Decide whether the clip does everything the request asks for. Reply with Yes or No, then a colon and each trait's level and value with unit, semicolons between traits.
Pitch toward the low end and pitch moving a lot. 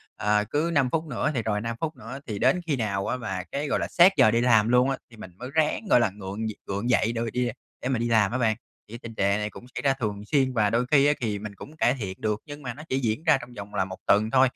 No: low, 115 Hz; average, 4.2 semitones